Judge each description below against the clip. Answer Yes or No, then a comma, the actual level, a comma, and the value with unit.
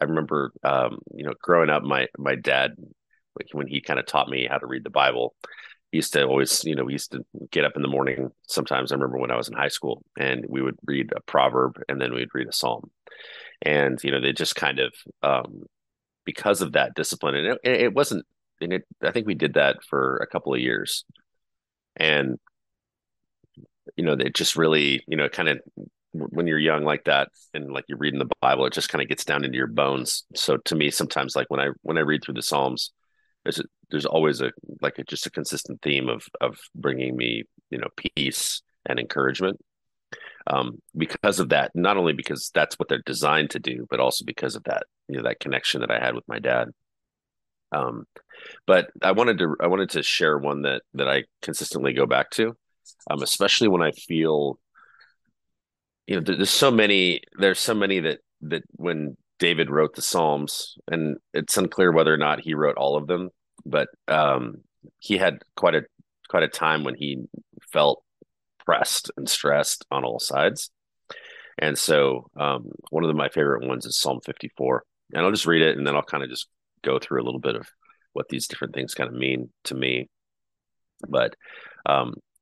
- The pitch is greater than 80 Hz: No, very low, 70 Hz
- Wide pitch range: No, average, 3.2 semitones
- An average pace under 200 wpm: No, fast, 205 wpm